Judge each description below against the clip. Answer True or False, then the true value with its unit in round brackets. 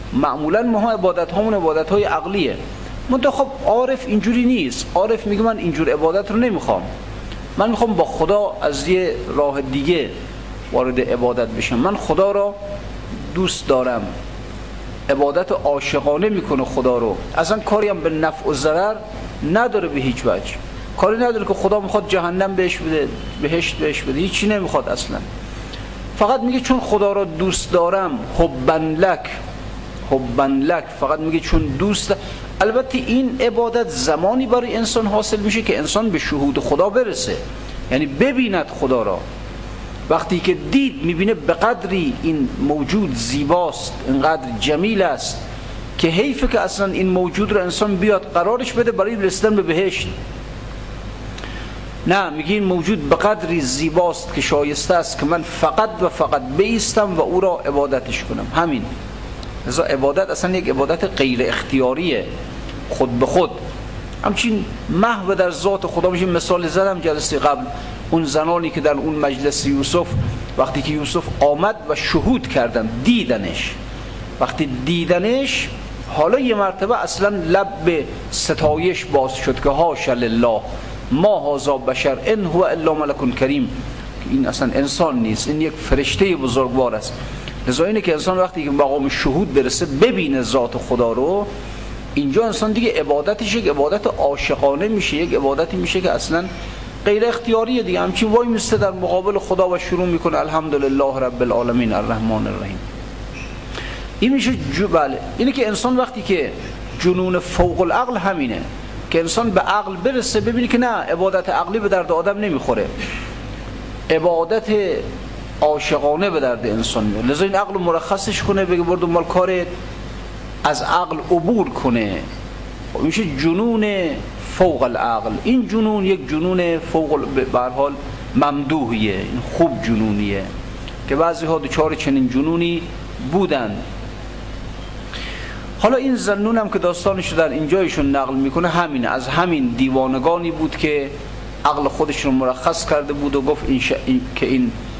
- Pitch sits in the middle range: True (170 Hz)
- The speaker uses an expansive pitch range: True (6.7 semitones)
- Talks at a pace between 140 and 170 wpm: True (145 wpm)